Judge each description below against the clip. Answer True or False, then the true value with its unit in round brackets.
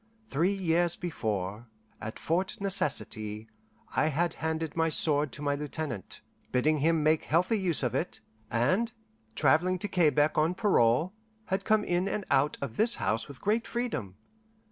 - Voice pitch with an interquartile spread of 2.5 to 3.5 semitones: False (5.1 semitones)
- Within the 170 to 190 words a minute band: False (155 wpm)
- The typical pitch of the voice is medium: True (160 Hz)